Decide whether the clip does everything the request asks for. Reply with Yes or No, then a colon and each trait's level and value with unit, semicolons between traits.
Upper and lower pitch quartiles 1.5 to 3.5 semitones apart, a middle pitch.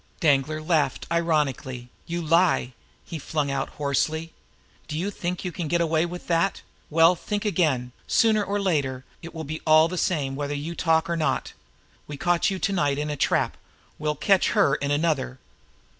Yes: average, 3.0 semitones; medium, 160 Hz